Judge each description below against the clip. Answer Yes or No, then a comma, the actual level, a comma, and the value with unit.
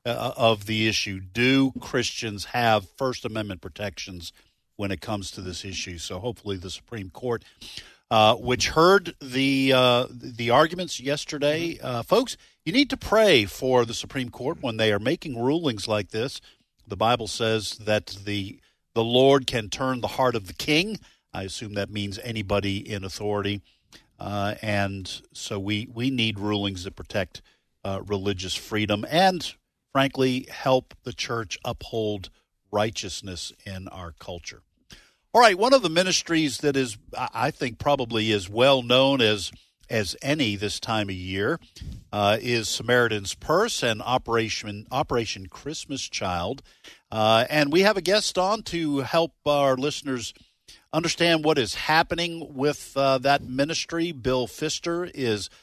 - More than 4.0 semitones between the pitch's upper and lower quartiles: Yes, average, 5.2 semitones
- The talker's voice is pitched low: Yes, low, 115 Hz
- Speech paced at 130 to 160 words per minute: Yes, average, 150 wpm